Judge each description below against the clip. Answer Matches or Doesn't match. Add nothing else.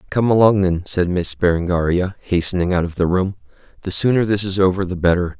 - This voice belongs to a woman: Doesn't match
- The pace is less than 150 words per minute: Doesn't match